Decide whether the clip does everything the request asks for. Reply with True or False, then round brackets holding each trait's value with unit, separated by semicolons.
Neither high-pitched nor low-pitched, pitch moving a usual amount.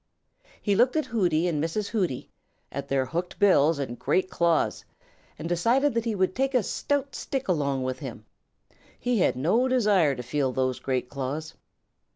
False (170 Hz; 8.4 semitones)